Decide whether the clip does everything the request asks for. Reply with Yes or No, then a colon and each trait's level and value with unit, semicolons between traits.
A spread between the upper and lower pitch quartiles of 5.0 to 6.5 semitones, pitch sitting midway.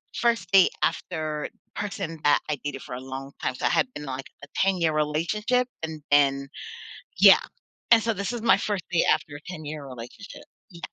Yes: wide, 5.6 semitones; medium, 155 Hz